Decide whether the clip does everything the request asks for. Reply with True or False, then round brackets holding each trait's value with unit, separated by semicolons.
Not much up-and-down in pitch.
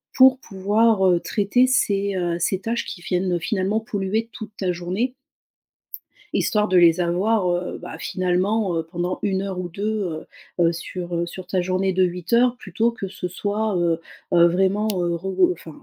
False (3.1 semitones)